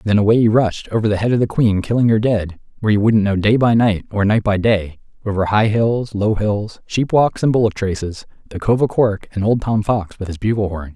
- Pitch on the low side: Yes, low, 105 Hz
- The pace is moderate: No, fast, 250 wpm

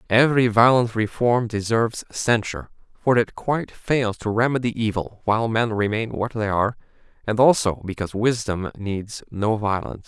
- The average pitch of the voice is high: No, low, 110 Hz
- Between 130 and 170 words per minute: Yes, average, 150 wpm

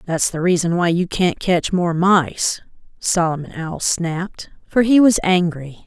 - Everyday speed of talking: Yes, average, 165 wpm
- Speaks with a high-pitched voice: No, medium, 175 Hz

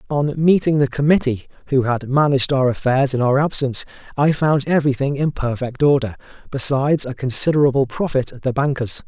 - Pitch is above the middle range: No, low, 135 Hz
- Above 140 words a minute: Yes, average, 165 wpm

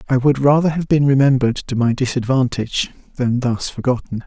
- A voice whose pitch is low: Yes, low, 130 Hz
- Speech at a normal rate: Yes, average, 170 wpm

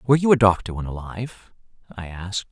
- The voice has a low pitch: Yes, low, 105 Hz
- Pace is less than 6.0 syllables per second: No, 6.3 syllables/s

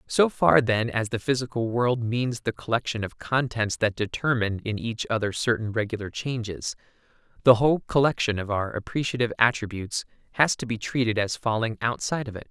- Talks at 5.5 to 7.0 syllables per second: Yes, 5.6 syllables/s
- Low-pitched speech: Yes, low, 115 Hz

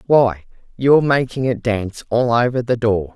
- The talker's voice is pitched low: Yes, low, 115 Hz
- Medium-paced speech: Yes, average, 170 wpm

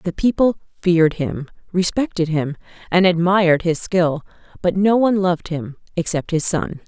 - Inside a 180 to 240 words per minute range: No, average, 155 wpm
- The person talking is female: Yes, female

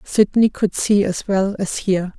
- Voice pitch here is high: Yes, high, 195 Hz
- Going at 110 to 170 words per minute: No, average, 190 wpm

